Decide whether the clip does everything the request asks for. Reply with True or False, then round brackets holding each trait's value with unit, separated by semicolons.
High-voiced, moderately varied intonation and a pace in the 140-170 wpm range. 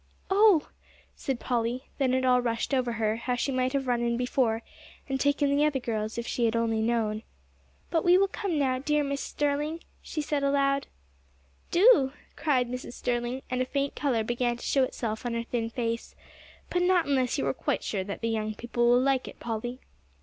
False (255 Hz; 3.1 semitones; 200 wpm)